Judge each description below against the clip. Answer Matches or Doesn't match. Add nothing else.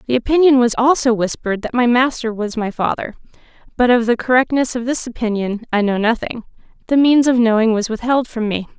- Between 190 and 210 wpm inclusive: Matches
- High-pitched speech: Matches